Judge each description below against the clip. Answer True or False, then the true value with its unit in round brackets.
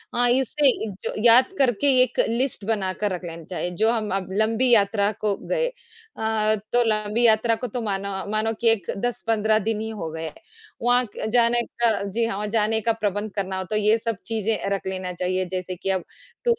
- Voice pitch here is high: True (220 Hz)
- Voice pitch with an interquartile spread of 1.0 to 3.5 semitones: True (2.8 semitones)